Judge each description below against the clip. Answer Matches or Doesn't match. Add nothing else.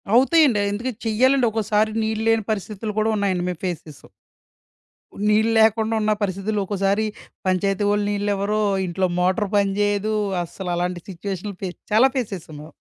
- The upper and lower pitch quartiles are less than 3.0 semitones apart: Matches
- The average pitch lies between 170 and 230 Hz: Matches